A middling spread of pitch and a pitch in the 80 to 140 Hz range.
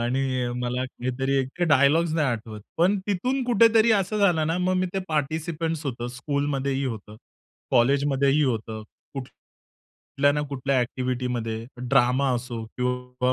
Yes: average, 4.2 semitones; low, 135 Hz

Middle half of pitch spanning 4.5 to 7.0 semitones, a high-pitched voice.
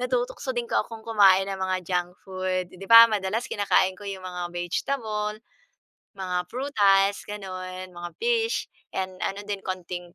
No: average, 3.0 semitones; high, 195 Hz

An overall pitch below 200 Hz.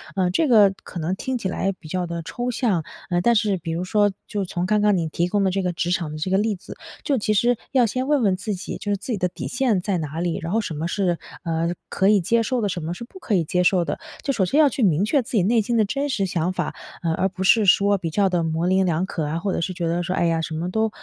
Yes: high, 190 Hz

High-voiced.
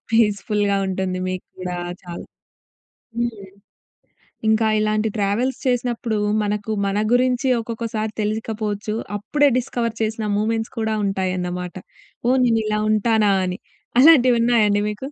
Yes: high, 215 Hz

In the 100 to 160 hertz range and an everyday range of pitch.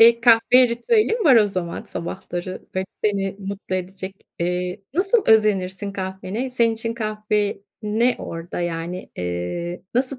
No: high, 200 Hz; average, 4.3 semitones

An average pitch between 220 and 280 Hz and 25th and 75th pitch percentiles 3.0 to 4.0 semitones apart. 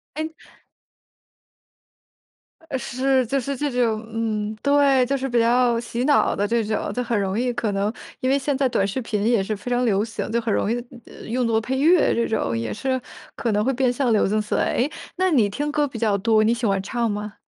Yes: high, 235 Hz; average, 3.4 semitones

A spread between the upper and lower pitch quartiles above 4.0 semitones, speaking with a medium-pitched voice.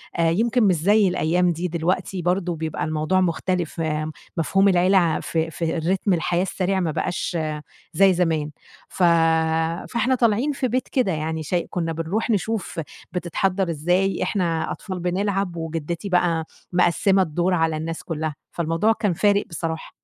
No: average, 3.0 semitones; medium, 175 Hz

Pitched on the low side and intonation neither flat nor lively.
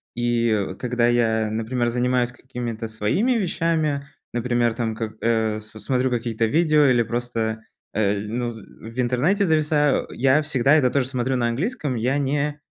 Yes: low, 120 Hz; average, 3.7 semitones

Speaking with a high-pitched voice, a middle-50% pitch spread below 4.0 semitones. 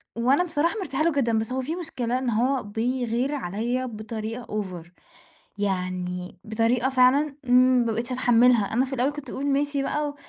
Yes: very high, 250 Hz; average, 3.6 semitones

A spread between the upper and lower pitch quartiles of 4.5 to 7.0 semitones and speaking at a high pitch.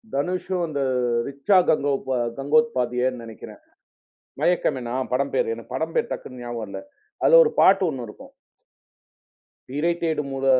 No: wide, 5.4 semitones; medium, 140 Hz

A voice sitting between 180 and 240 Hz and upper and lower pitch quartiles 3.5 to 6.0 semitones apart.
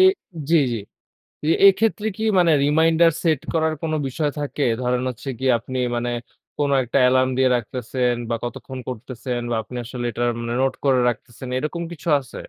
No: low, 130 Hz; average, 4.3 semitones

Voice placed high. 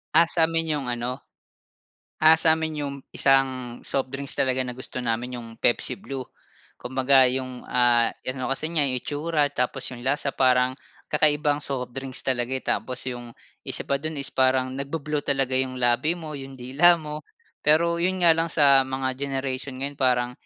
No: low, 135 Hz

